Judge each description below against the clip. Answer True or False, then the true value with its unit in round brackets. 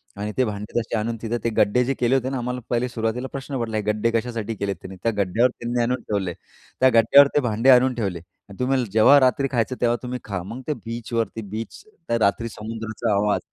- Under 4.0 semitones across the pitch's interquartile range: True (2.7 semitones)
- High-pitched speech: False (115 Hz)